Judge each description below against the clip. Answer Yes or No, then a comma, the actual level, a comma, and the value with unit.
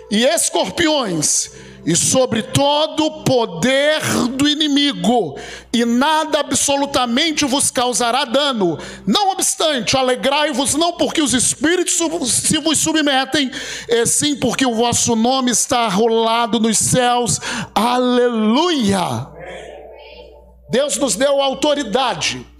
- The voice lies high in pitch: Yes, very high, 265 Hz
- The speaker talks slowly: Yes, slow, 105 wpm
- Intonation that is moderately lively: Yes, average, 3.9 semitones